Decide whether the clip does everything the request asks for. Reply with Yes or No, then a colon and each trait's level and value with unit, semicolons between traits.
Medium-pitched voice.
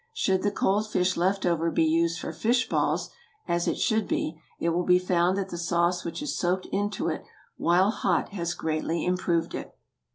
Yes: medium, 180 Hz